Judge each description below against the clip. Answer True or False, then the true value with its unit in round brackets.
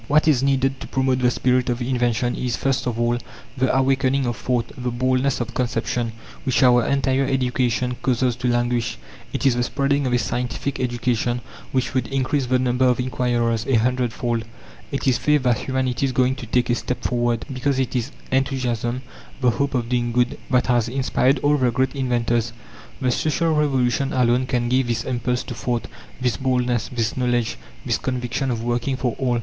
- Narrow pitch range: True (1.5 semitones)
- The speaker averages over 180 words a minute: True (190 wpm)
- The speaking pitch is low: True (125 Hz)